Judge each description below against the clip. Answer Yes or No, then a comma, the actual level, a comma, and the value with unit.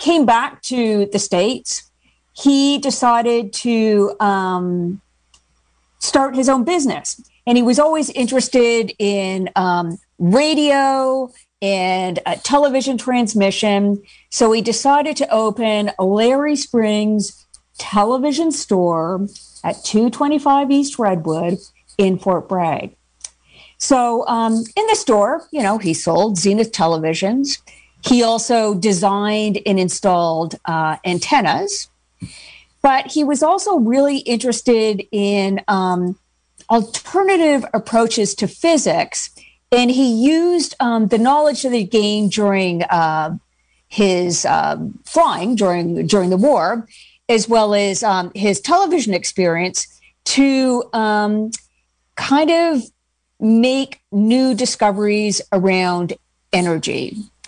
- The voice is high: Yes, high, 225 Hz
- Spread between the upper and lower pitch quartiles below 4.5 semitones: No, average, 5.3 semitones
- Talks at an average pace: No, slow, 110 wpm